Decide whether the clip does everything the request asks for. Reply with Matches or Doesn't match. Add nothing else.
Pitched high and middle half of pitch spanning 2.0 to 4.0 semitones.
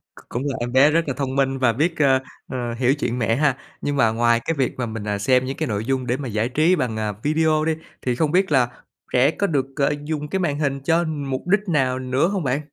Doesn't match